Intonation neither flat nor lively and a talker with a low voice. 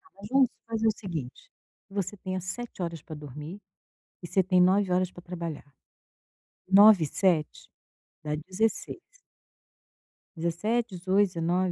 No: average, 3.3 semitones; medium, 185 Hz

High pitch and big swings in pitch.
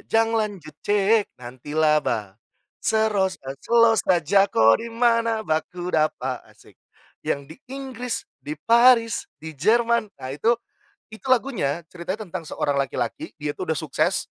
Yes: high, 195 Hz; wide, 7.0 semitones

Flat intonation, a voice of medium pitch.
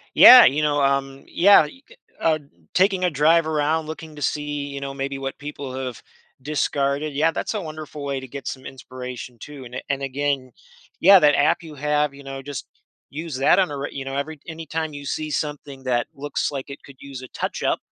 Yes: narrow, 2.2 semitones; medium, 145 Hz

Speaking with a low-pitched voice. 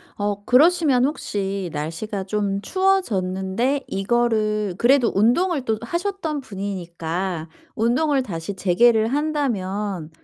No: high, 215 Hz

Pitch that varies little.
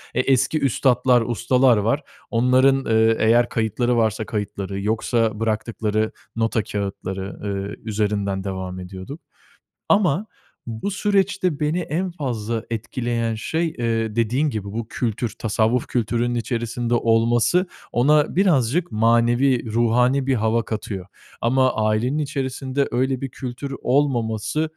No: average, 3.5 semitones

